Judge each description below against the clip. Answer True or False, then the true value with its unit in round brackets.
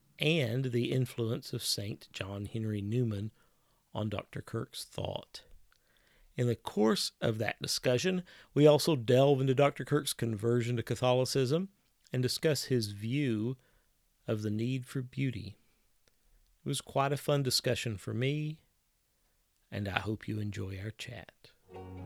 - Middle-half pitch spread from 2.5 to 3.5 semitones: False (4.0 semitones)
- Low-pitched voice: True (120 Hz)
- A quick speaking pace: False (140 wpm)